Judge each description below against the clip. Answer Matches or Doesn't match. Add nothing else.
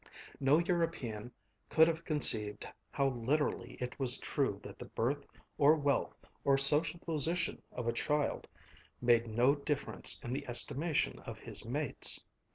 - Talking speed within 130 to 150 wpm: Matches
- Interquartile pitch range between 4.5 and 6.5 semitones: Doesn't match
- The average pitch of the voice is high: Doesn't match